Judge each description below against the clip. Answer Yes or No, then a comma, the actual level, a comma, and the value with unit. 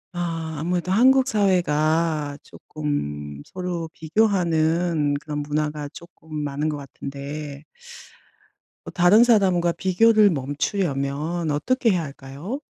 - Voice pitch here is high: No, medium, 160 Hz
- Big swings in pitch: No, average, 3.8 semitones